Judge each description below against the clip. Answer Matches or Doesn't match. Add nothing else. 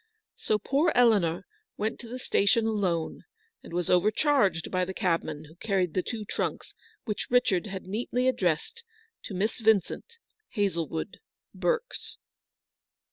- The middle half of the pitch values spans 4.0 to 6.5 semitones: Matches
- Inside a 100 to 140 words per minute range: Matches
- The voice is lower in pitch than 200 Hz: Doesn't match